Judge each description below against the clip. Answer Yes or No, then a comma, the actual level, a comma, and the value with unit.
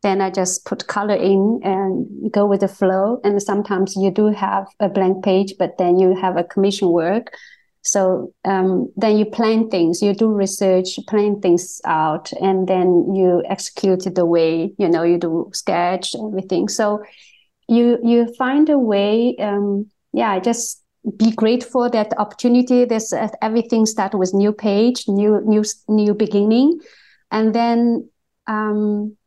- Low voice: No, high, 205 Hz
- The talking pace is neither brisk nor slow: Yes, average, 160 wpm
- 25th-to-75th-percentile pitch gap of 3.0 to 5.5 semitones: No, narrow, 2.6 semitones